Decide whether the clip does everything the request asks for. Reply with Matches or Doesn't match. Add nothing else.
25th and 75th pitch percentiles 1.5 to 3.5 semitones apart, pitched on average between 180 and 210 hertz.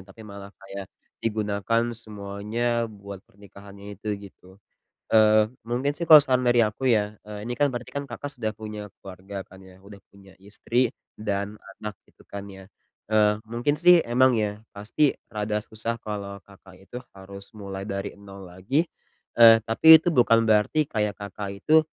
Doesn't match